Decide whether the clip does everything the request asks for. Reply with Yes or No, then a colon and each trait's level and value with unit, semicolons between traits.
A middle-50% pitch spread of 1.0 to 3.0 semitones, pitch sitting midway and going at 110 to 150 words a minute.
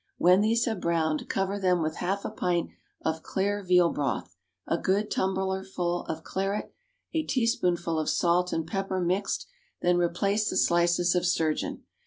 No: narrow, 2.4 semitones; medium, 180 Hz; average, 160 wpm